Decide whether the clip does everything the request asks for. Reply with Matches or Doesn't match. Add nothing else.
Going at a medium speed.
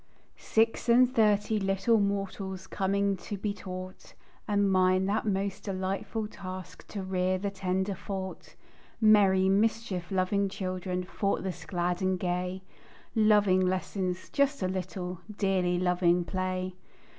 Doesn't match